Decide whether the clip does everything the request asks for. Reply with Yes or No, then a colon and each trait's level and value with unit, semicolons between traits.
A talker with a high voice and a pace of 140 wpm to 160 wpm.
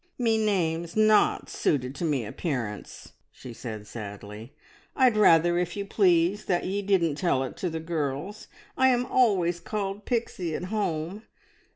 No: medium, 175 Hz; average, 155 wpm